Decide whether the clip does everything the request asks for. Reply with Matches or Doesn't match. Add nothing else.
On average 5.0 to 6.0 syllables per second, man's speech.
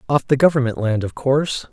Matches